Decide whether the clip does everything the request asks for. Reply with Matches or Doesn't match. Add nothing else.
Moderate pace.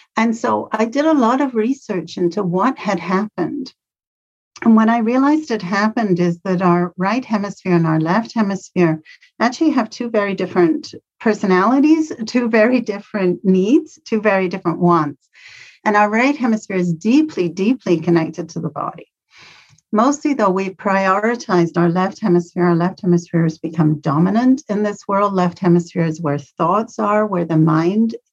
Matches